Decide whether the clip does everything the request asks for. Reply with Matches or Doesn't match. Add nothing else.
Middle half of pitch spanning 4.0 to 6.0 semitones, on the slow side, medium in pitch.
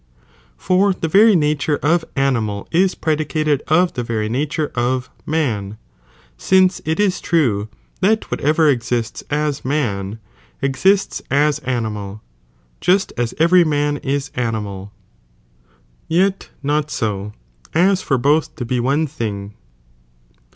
Matches